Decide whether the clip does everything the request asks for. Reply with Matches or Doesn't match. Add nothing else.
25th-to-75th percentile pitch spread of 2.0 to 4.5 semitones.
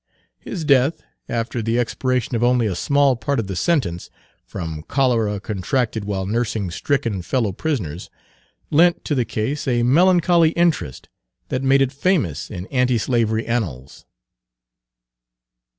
Doesn't match